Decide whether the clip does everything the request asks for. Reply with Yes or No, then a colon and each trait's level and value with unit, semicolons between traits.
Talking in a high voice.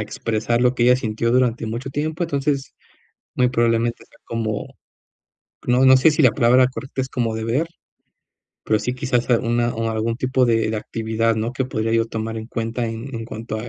No: low, 120 Hz